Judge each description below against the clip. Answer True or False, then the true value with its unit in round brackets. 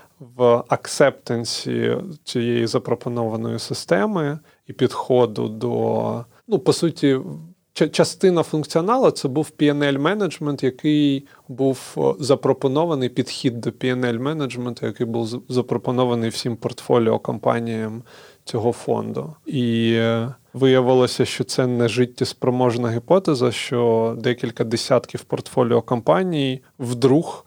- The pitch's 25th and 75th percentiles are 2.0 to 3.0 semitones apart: False (3.4 semitones)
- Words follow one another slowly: True (100 wpm)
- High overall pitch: False (125 Hz)